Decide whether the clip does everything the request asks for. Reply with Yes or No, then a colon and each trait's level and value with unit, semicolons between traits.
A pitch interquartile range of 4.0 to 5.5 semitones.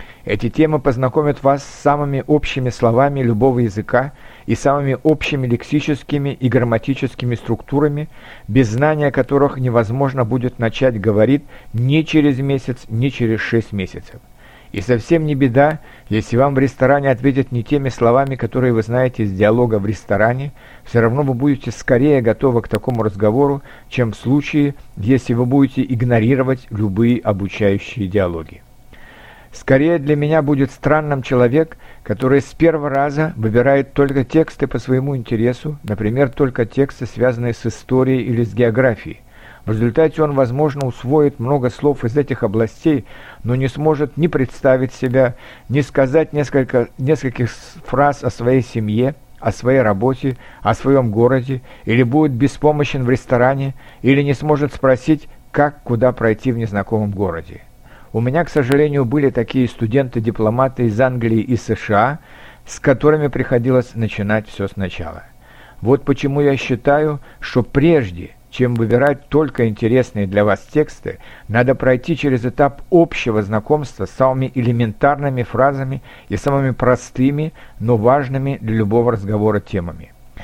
No: average, 3.2 semitones